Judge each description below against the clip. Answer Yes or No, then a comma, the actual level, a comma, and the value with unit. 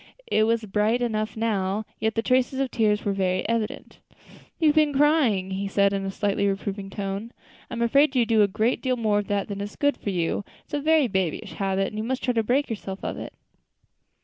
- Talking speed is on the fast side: Yes, fast, 230 wpm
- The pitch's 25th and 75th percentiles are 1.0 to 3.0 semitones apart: No, average, 3.6 semitones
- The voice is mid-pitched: No, high, 215 Hz